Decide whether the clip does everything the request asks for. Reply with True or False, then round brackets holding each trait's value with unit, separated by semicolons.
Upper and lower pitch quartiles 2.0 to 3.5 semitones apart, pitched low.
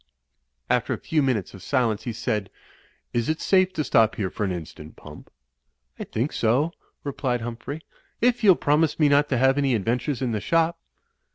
False (5.2 semitones; 130 Hz)